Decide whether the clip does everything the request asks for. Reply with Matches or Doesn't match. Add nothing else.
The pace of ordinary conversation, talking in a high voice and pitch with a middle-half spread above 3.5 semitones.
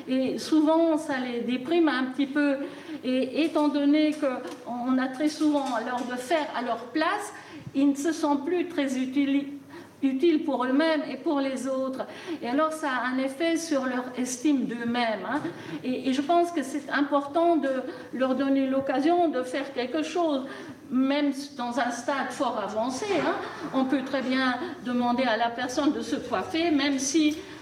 Doesn't match